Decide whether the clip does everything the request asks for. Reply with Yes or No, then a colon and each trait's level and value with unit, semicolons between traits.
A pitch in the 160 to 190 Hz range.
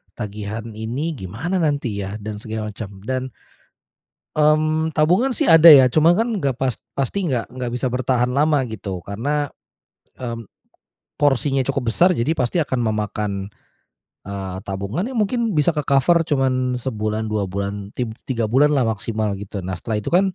No: low, 125 Hz